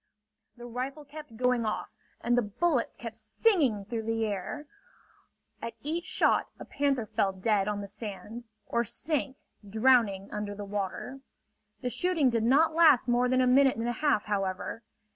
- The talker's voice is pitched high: Yes, high, 235 Hz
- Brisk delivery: No, average, 165 wpm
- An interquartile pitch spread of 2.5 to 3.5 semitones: No, average, 4.3 semitones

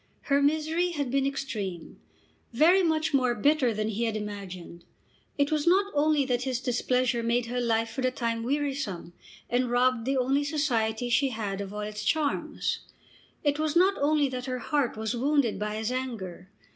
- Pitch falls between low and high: No, very high, 255 Hz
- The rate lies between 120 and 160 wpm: No, average, 180 wpm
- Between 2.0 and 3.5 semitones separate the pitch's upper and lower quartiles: No, average, 4.4 semitones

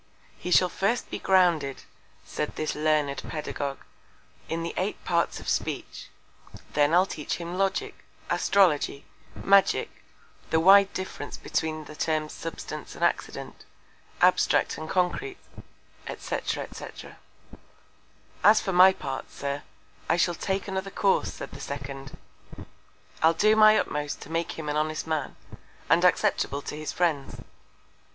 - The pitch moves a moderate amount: Yes, average, 4.1 semitones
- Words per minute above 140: No, slow, 135 wpm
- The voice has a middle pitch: Yes, medium, 165 Hz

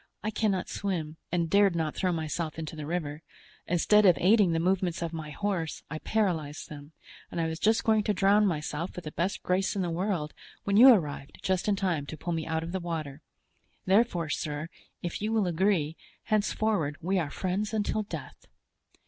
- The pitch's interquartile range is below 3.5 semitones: No, average, 4.1 semitones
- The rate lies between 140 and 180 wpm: No, average, 195 wpm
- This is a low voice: No, medium, 175 Hz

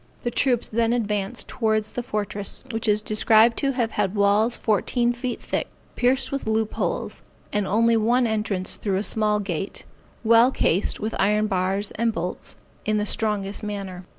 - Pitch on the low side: No, high, 215 Hz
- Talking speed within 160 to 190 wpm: Yes, average, 170 wpm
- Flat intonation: Yes, narrow, 2.3 semitones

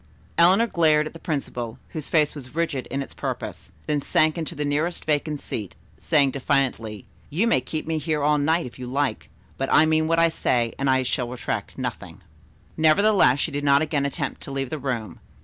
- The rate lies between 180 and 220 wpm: Yes, average, 200 wpm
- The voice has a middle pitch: Yes, medium, 145 Hz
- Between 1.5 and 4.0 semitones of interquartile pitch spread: Yes, average, 2.9 semitones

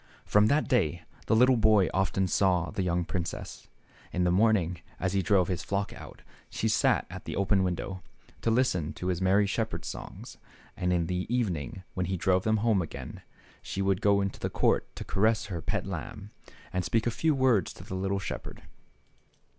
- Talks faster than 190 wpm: Yes, average, 200 wpm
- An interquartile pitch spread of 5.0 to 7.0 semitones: No, average, 3.1 semitones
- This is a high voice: No, very low, 95 Hz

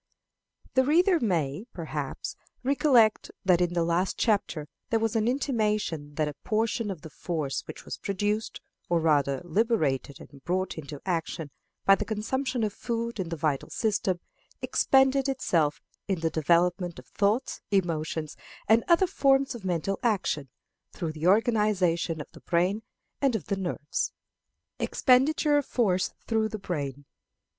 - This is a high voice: Yes, high, 195 Hz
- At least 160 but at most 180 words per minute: No, average, 150 wpm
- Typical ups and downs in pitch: No, wide, 6.0 semitones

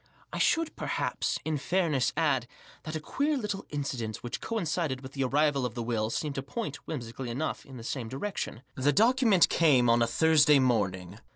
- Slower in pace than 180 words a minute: No, average, 185 wpm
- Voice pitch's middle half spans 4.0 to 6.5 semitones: Yes, average, 5.0 semitones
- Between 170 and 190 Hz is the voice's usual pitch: No, medium, 140 Hz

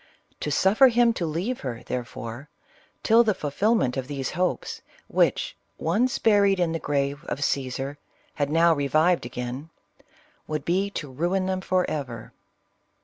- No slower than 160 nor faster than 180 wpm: No, average, 145 wpm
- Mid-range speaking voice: Yes, medium, 160 Hz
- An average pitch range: No, wide, 5.8 semitones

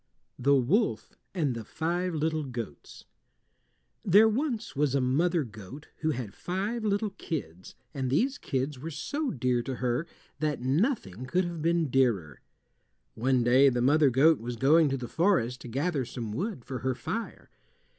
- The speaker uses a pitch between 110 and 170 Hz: Yes, medium, 140 Hz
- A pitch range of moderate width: No, wide, 5.7 semitones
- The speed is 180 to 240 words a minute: No, average, 165 wpm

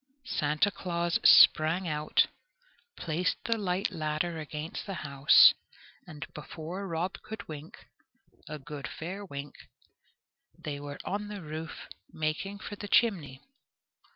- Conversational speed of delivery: No, slow, 125 wpm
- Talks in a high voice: No, medium, 160 Hz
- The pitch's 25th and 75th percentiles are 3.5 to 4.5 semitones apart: Yes, average, 4.0 semitones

